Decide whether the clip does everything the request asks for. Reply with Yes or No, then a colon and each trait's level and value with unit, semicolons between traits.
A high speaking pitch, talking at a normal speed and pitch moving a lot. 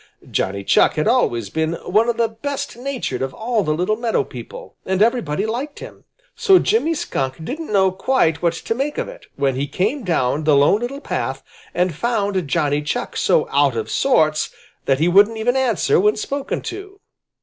Yes: high, 200 Hz; average, 190 wpm; wide, 8.5 semitones